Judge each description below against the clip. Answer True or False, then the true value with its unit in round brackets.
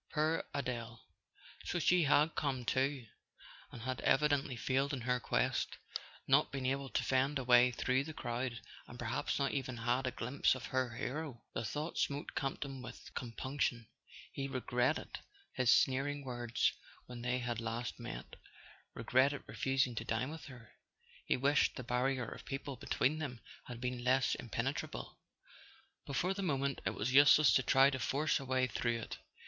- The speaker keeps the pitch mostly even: True (2.3 semitones)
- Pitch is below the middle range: True (130 Hz)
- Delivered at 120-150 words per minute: False (170 wpm)